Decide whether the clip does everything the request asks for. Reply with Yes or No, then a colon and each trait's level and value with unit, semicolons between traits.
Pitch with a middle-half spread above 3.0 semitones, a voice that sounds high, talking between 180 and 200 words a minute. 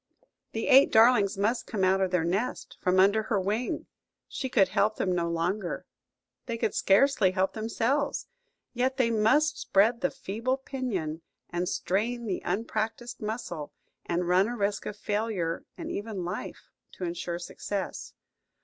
No: average, 4.0 semitones; high, 210 Hz; average, 150 wpm